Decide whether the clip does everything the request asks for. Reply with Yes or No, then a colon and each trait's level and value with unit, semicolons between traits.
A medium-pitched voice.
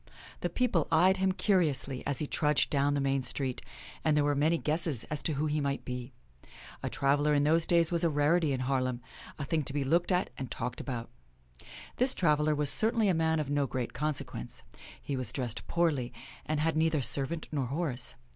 Yes: medium, 150 Hz